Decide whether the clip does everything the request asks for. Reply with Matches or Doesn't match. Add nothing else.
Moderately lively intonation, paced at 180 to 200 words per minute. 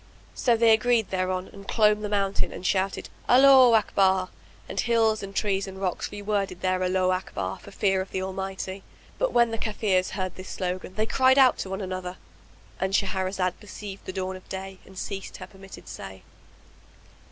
Doesn't match